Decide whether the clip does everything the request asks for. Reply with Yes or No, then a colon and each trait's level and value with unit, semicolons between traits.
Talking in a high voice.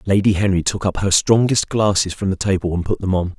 No: very low, 95 Hz